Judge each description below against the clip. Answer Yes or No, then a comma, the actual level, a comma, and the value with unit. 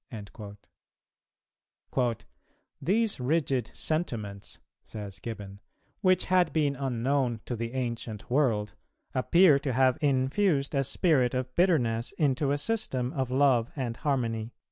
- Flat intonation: No, average, 4.0 semitones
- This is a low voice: Yes, low, 130 Hz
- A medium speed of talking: No, slow, 120 wpm